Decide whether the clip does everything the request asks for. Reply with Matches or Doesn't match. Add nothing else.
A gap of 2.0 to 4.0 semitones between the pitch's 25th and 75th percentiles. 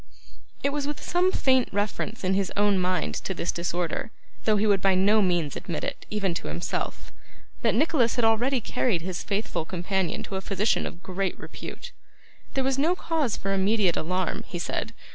Doesn't match